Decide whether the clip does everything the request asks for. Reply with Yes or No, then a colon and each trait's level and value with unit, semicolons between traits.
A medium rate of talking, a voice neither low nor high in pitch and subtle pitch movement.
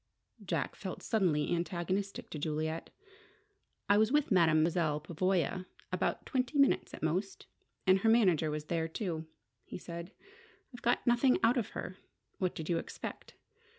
No: average, 150 wpm; medium, 180 Hz; average, 4.9 semitones